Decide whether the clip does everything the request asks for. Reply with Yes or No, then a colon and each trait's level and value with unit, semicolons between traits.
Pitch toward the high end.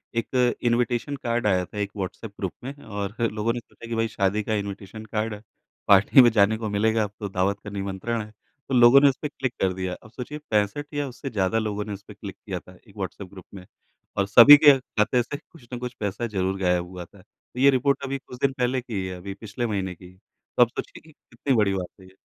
No: low, 110 Hz